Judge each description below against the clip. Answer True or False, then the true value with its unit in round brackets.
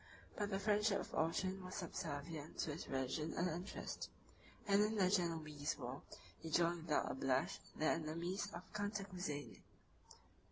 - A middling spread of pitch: True (4.1 semitones)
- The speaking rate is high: False (150 wpm)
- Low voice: False (170 Hz)